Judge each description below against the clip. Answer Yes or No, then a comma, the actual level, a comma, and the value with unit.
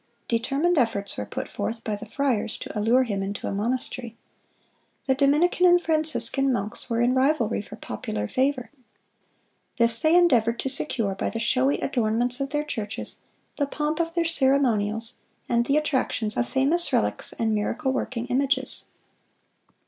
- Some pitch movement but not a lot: Yes, average, 4.0 semitones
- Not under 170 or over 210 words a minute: No, average, 155 wpm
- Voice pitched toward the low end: No, very high, 255 Hz